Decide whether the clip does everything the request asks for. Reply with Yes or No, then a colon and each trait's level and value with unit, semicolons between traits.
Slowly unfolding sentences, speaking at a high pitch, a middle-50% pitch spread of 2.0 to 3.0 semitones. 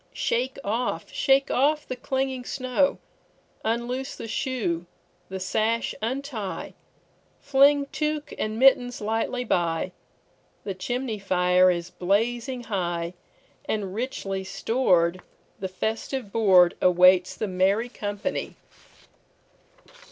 No: slow, 90 wpm; high, 220 Hz; wide, 5.5 semitones